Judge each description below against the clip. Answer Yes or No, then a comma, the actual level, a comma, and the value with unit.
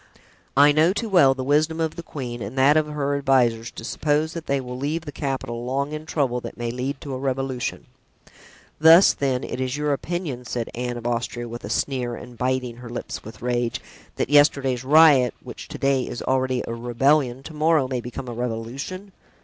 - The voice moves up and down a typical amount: Yes, average, 3.3 semitones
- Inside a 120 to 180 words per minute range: No, fast, 205 wpm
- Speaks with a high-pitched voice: No, low, 130 Hz